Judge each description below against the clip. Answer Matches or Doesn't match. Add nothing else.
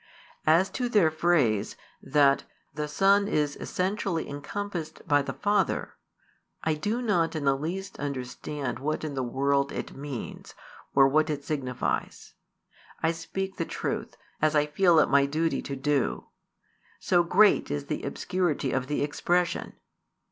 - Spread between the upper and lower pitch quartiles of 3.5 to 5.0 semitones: Matches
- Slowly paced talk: Doesn't match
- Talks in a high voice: Doesn't match